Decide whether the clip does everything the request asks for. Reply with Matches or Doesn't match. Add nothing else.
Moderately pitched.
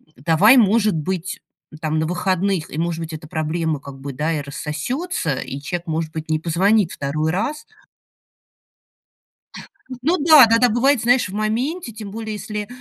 Matches